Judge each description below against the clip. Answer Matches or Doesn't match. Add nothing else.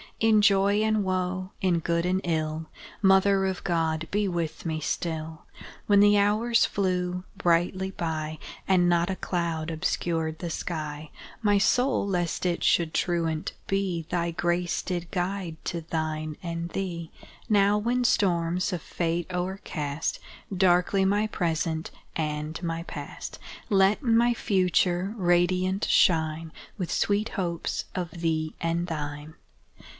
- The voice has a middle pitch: Matches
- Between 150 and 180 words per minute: Doesn't match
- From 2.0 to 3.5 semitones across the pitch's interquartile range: Matches